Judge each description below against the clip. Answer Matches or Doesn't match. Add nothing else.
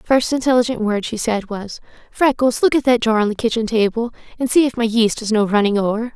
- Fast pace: Matches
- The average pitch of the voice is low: Doesn't match